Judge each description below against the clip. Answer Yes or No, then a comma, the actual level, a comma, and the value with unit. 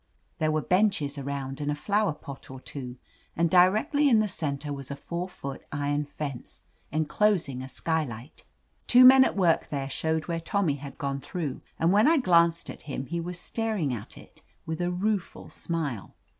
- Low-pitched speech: No, medium, 160 Hz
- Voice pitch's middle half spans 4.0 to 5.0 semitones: Yes, average, 4.7 semitones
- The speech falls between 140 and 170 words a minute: No, average, 185 wpm